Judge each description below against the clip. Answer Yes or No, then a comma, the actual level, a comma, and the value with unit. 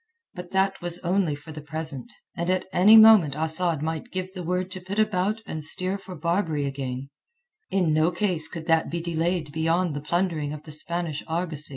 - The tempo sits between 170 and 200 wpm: Yes, average, 195 wpm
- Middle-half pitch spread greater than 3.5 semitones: No, average, 2.9 semitones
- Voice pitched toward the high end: No, medium, 170 Hz